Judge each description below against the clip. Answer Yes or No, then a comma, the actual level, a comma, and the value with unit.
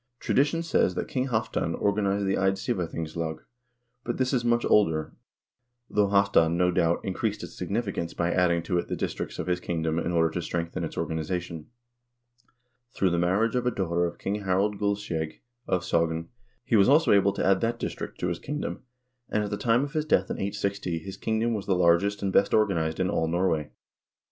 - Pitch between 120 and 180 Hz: No, very low, 95 Hz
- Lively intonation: No, average, 3.7 semitones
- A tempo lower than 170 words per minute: No, average, 195 wpm